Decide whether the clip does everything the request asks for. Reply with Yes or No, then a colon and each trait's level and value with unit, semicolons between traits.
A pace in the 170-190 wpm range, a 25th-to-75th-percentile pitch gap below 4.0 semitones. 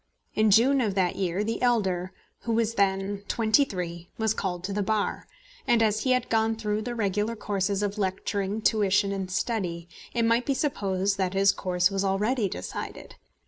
Yes: average, 185 wpm; average, 2.7 semitones